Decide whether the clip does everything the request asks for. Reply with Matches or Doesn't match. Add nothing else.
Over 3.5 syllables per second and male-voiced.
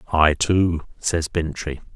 Doesn't match